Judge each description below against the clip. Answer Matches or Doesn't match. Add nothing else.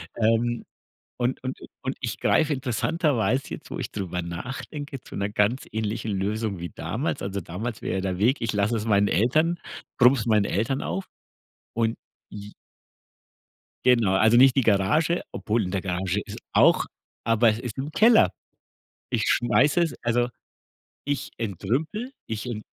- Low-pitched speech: Matches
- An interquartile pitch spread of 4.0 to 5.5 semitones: Matches